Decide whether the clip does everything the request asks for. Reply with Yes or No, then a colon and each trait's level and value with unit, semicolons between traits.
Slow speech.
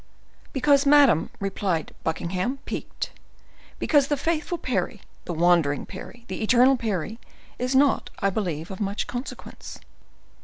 Yes: slow, 125 wpm